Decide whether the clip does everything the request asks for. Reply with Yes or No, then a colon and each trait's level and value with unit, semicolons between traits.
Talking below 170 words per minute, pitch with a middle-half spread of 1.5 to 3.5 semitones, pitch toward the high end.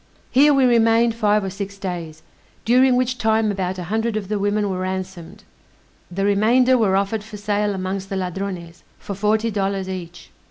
No: average, 175 wpm; average, 2.9 semitones; high, 200 Hz